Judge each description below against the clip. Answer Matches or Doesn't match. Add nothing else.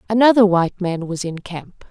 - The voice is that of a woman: Matches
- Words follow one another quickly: Doesn't match